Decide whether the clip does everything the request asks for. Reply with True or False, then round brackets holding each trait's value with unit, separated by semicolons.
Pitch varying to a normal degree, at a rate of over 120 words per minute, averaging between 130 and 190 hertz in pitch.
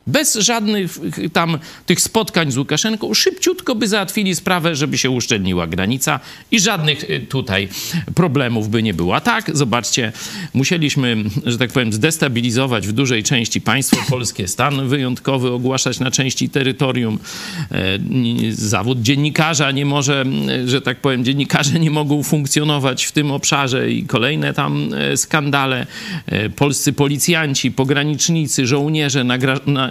True (4.0 semitones; 130 wpm; 140 Hz)